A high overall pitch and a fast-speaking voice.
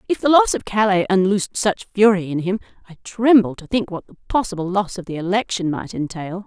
Yes: high, 195 Hz; fast, 215 wpm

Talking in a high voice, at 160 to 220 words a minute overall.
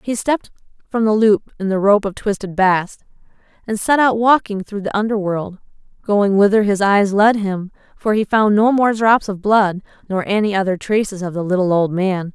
Yes: high, 205 Hz; average, 200 wpm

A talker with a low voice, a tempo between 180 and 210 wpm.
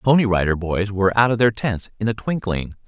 No: low, 105 Hz; fast, 250 wpm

